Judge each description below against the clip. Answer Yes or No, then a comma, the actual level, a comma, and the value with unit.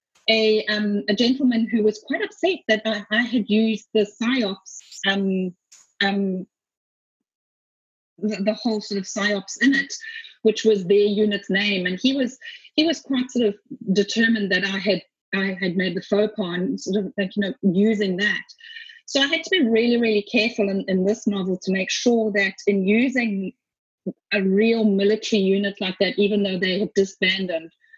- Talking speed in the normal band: Yes, average, 180 wpm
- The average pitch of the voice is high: Yes, high, 210 Hz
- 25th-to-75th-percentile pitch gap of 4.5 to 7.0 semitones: No, average, 2.8 semitones